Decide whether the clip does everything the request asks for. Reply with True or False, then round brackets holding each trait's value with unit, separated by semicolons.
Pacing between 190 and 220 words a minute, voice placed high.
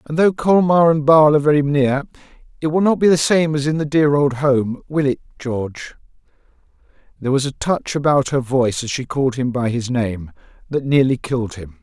False (205 wpm; 140 Hz)